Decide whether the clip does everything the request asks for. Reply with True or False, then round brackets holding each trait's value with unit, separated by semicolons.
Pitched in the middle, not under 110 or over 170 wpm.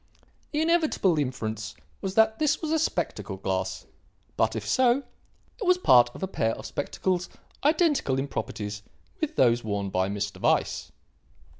True (180 Hz; 155 wpm)